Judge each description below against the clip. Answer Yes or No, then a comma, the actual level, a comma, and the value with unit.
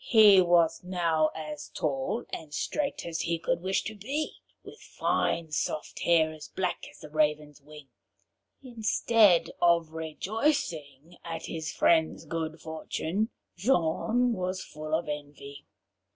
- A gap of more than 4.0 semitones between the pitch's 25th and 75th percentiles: No, average, 3.6 semitones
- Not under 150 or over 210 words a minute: No, slow, 135 wpm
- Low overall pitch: No, medium, 165 Hz